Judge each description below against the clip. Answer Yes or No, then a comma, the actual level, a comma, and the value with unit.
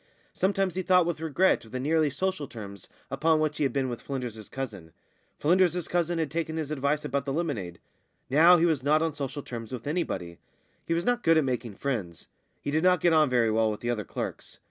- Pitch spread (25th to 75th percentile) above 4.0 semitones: Yes, wide, 5.4 semitones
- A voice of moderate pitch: Yes, medium, 145 Hz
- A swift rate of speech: Yes, fast, 220 wpm